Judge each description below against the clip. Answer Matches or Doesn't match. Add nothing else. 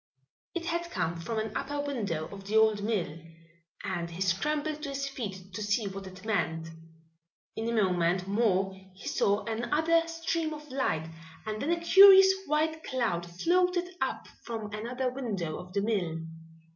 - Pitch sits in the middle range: Doesn't match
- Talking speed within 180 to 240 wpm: Doesn't match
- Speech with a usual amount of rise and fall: Doesn't match